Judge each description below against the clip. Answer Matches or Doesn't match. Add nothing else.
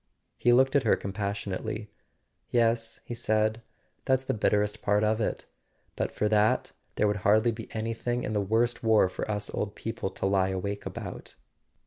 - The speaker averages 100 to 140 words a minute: Doesn't match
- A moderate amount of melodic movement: Doesn't match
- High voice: Doesn't match